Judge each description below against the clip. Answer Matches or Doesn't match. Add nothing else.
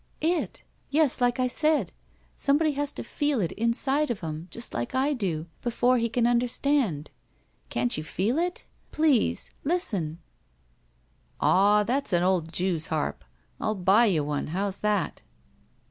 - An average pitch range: Doesn't match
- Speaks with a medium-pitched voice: Doesn't match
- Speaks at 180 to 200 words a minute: Doesn't match